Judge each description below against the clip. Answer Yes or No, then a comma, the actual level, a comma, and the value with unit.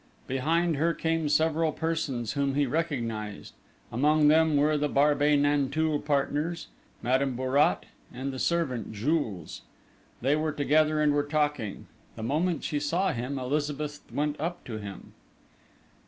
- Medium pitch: Yes, medium, 145 Hz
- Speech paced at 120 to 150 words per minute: Yes, average, 140 wpm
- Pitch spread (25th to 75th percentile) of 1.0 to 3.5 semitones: Yes, average, 2.8 semitones